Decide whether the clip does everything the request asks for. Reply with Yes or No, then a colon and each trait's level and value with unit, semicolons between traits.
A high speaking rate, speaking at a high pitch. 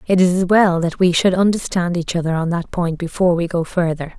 No: fast, 245 wpm; medium, 175 Hz